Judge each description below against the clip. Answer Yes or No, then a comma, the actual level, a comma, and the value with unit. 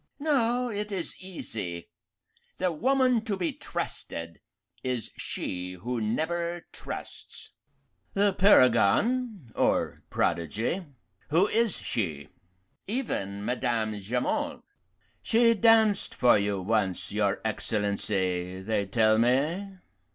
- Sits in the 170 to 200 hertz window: No, low, 125 Hz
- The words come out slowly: Yes, slow, 100 wpm